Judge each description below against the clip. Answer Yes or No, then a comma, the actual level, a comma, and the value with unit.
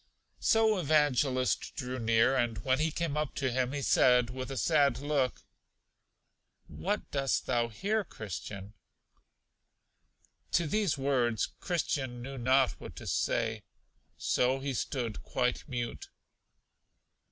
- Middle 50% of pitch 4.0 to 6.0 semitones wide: No, average, 3.4 semitones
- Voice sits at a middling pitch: No, low, 130 Hz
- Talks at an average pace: No, slow, 125 wpm